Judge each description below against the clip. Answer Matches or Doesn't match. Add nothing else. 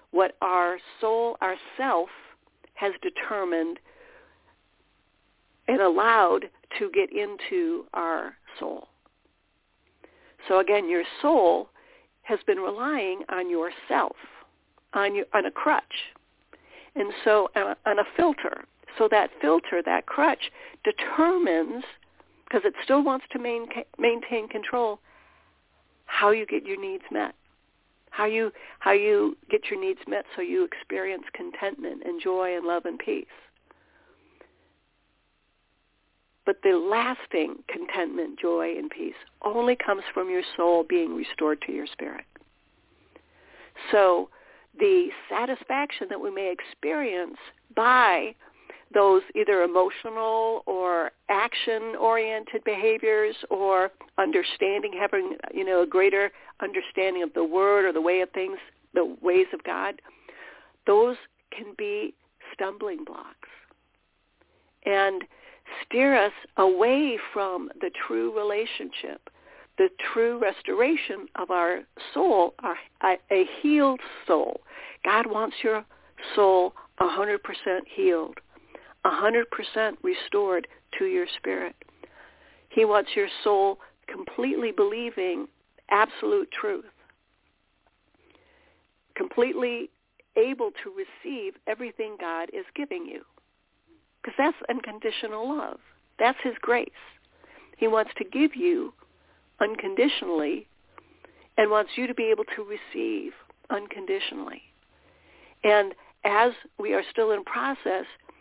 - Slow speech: Matches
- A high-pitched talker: Matches